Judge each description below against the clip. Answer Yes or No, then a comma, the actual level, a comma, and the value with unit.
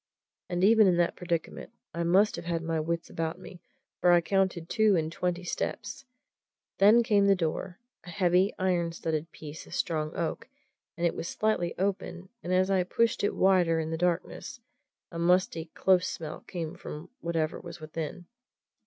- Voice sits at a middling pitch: Yes, medium, 175 Hz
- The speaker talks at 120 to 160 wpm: No, average, 175 wpm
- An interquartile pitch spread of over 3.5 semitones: No, narrow, 2.4 semitones